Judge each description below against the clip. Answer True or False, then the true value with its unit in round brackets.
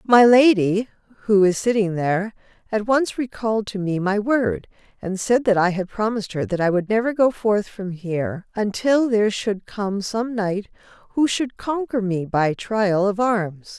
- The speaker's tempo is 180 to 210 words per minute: True (185 wpm)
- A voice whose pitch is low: False (210 Hz)